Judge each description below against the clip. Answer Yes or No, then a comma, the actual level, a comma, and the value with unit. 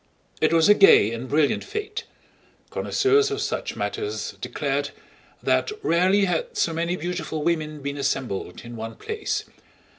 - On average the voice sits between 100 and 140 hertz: No, medium, 170 Hz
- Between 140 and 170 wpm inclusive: Yes, average, 145 wpm